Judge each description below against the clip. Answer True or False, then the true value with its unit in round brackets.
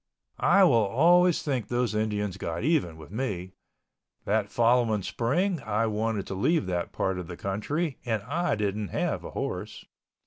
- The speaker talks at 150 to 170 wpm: True (165 wpm)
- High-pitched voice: False (110 Hz)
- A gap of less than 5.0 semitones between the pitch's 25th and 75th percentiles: False (5.5 semitones)